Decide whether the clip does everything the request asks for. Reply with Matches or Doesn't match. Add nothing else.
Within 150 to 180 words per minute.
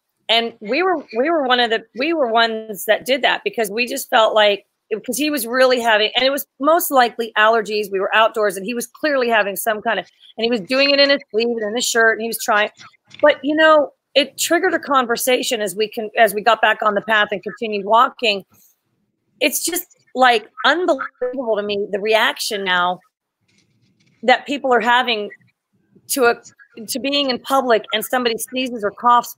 Doesn't match